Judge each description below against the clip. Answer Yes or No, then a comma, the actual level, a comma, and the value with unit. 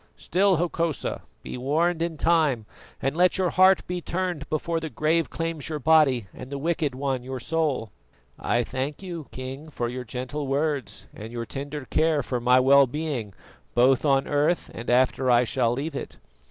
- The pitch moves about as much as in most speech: Yes, average, 4.2 semitones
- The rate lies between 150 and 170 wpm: No, average, 180 wpm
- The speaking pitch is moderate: Yes, medium, 145 Hz